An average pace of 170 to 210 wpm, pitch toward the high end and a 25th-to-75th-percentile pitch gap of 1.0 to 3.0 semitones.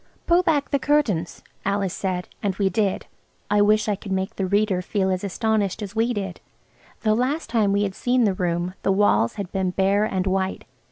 Yes: fast, 205 wpm; high, 200 Hz; narrow, 2.5 semitones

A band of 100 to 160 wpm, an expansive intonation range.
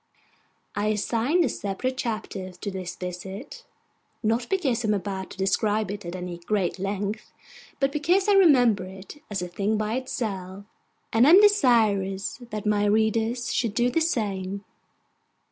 No: average, 155 wpm; average, 4.2 semitones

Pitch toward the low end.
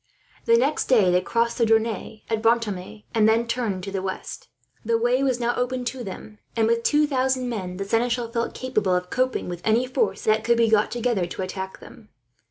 No: high, 230 Hz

